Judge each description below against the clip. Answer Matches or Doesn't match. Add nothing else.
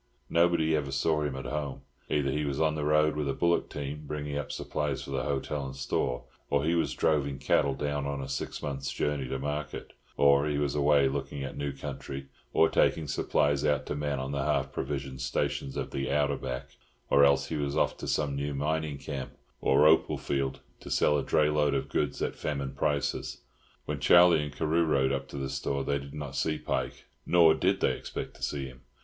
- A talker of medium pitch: Doesn't match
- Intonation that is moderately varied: Doesn't match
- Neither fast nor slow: Doesn't match